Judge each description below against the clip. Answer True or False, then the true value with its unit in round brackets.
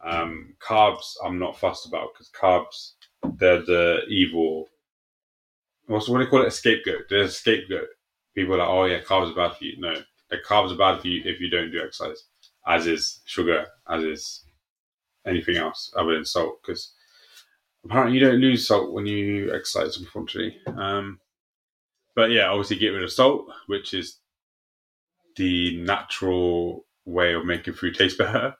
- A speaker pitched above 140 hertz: False (95 Hz)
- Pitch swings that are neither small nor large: False (5.8 semitones)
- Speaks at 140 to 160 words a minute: False (170 wpm)